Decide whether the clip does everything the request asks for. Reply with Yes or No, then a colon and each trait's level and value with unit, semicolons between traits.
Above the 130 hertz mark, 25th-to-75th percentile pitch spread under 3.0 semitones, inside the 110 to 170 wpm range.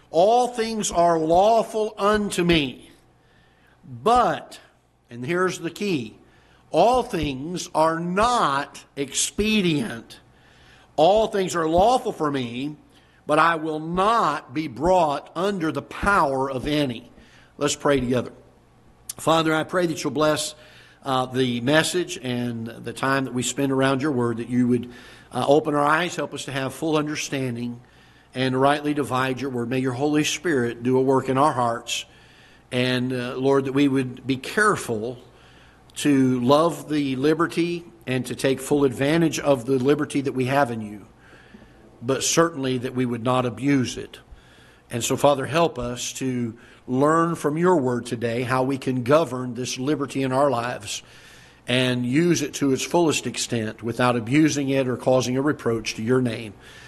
No: medium, 140 Hz; average, 3.9 semitones; average, 160 wpm